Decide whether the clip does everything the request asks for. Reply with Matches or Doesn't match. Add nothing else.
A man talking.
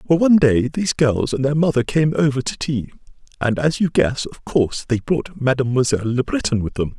Matches